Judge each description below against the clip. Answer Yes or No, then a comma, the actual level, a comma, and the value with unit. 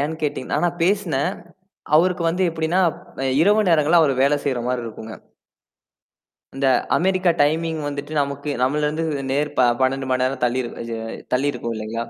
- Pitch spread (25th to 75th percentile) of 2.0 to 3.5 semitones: No, average, 4.1 semitones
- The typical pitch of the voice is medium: Yes, medium, 145 Hz